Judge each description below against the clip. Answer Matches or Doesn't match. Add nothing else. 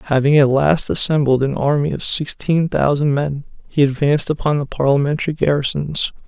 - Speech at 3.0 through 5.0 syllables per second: Doesn't match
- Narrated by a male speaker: Matches